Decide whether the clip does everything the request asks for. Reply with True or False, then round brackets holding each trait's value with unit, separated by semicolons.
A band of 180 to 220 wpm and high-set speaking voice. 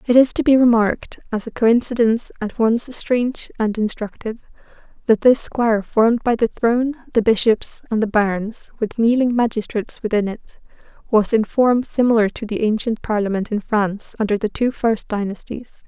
False (170 wpm; 225 Hz)